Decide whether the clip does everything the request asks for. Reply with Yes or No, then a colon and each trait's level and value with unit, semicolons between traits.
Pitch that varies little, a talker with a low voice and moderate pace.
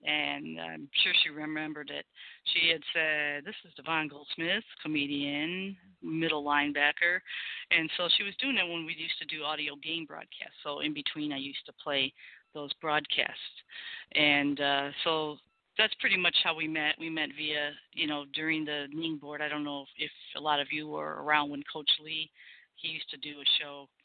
No: narrow, 2.0 semitones; medium, 150 Hz; average, 190 wpm